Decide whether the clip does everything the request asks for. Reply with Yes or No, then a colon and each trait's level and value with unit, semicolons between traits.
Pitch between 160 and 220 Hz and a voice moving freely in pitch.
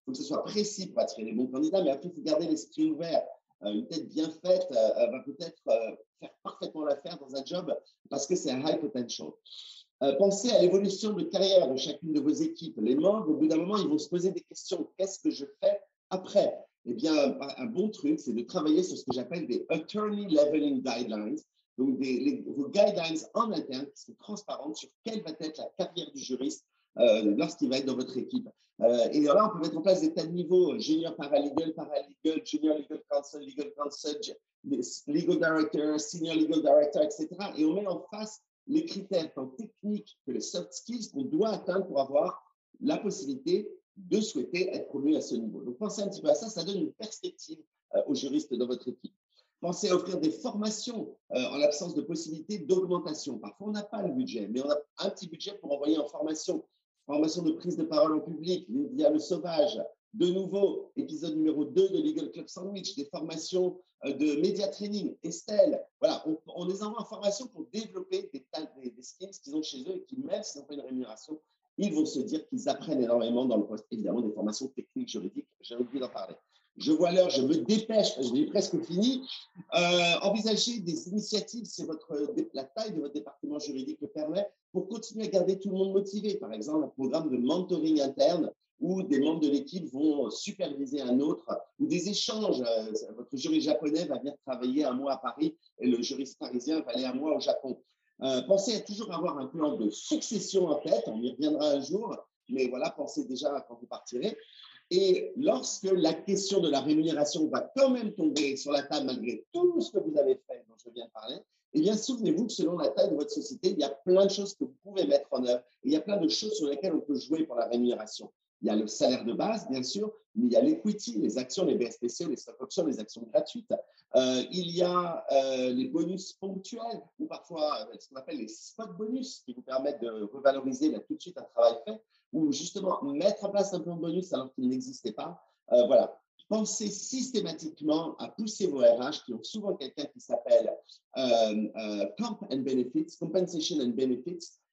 Yes: medium, 185 Hz; wide, 8.6 semitones